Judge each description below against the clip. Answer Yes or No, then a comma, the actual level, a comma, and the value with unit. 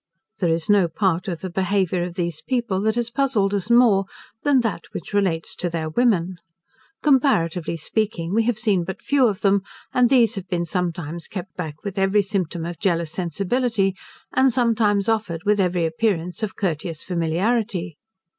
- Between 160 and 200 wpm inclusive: Yes, average, 175 wpm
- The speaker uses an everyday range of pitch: Yes, average, 4.3 semitones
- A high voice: Yes, high, 195 Hz